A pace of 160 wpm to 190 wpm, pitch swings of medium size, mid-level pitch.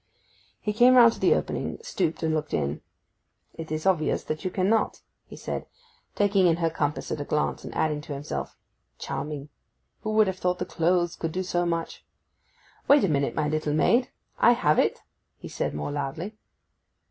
Yes: average, 180 wpm; average, 4.2 semitones; medium, 165 Hz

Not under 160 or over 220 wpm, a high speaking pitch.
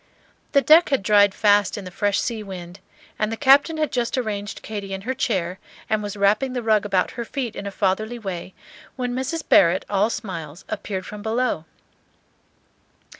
Yes: average, 180 wpm; high, 210 Hz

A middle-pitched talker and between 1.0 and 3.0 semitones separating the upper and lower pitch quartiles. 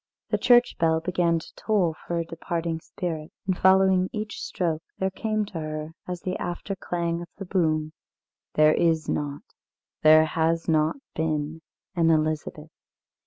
Yes: medium, 165 Hz; narrow, 2.6 semitones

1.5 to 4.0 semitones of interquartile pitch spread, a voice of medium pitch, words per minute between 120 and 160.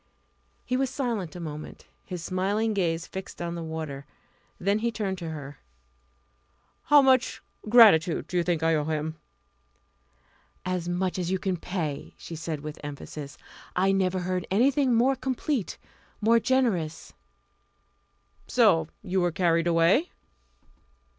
No: average, 5.0 semitones; medium, 180 Hz; average, 140 wpm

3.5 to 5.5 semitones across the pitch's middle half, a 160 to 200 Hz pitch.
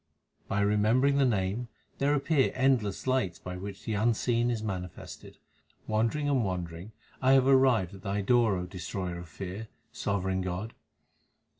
No: average, 5.2 semitones; low, 105 Hz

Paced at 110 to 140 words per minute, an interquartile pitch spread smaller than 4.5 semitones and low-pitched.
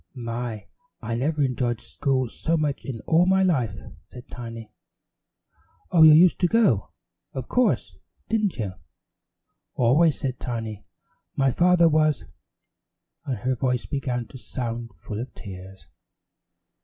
No: slow, 135 wpm; average, 5.2 semitones; low, 130 Hz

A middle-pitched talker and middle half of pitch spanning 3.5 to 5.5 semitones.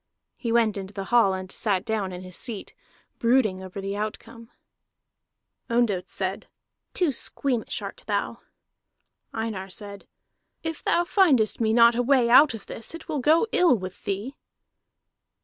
No: high, 225 Hz; average, 4.5 semitones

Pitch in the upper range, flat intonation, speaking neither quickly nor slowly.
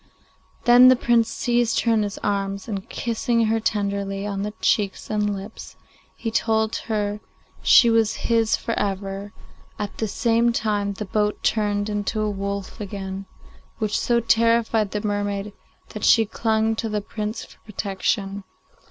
Yes: high, 210 Hz; narrow, 2.0 semitones; average, 155 wpm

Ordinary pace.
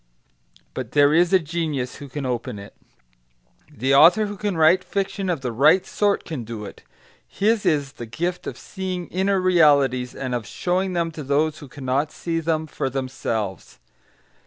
Yes: average, 175 wpm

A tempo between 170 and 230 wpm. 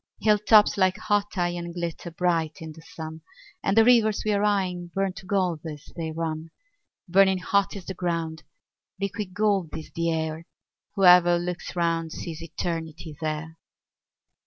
No: average, 155 wpm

